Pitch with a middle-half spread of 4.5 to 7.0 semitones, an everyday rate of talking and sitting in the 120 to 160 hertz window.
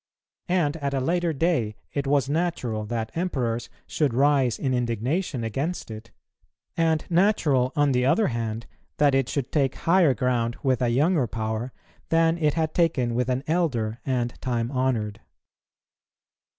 Yes: average, 5.1 semitones; average, 150 wpm; low, 135 Hz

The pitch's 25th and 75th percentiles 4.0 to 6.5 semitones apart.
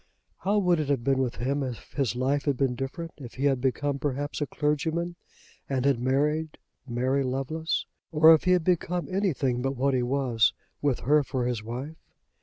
No: average, 3.3 semitones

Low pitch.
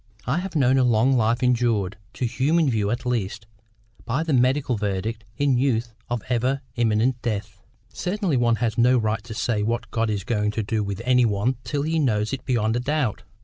Yes: low, 120 Hz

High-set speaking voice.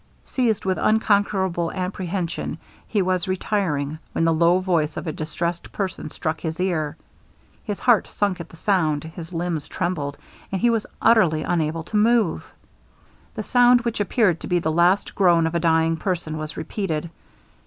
No: medium, 175 Hz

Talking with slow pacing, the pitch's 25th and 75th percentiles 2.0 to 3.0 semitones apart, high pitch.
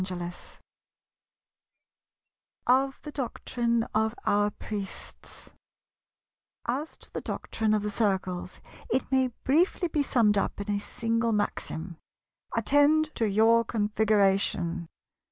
No: slow, 115 wpm; average, 4.0 semitones; high, 220 Hz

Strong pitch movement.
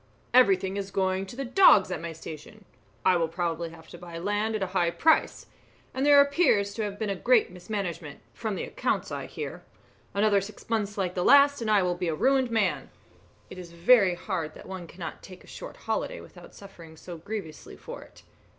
No: average, 4.0 semitones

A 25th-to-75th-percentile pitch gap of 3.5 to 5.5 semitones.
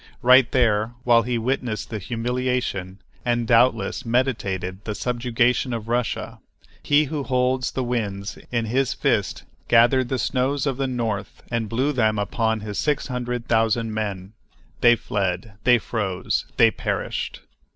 No: average, 2.7 semitones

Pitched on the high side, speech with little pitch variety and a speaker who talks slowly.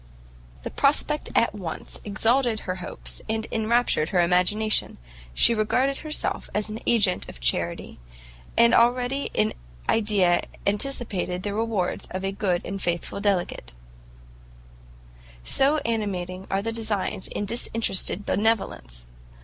No: high, 210 Hz; average, 4.0 semitones; slow, 125 wpm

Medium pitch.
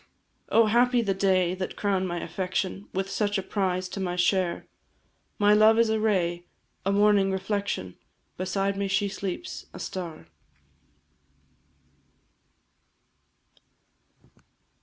No: high, 195 Hz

